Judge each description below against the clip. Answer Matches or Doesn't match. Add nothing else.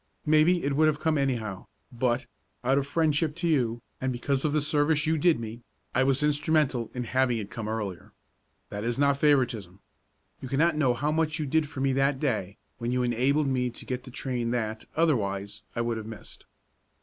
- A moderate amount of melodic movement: Matches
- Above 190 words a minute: Matches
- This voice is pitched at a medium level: Doesn't match